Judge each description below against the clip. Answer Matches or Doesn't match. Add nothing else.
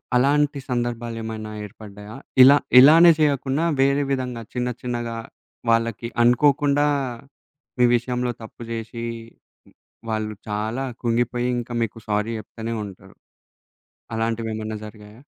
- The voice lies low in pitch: Matches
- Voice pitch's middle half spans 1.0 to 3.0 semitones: Matches